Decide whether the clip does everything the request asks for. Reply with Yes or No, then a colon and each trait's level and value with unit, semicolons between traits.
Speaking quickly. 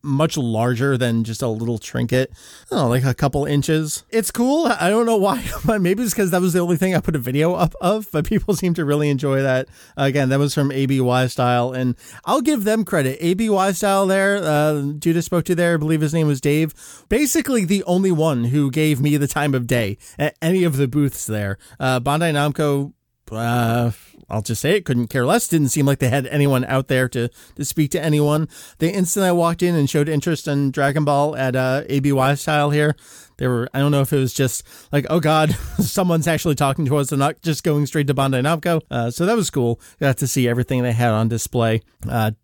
Yes: fast, 230 wpm